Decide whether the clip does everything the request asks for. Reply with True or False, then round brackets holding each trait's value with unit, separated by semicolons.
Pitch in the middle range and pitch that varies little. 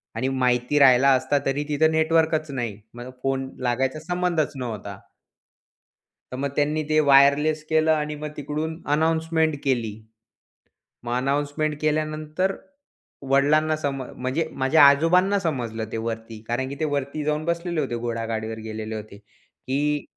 False (145 Hz; 3.7 semitones)